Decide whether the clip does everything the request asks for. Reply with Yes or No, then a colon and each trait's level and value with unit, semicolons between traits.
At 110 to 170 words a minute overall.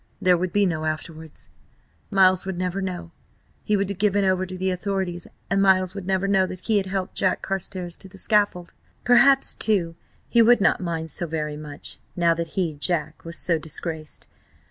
No: average, 190 wpm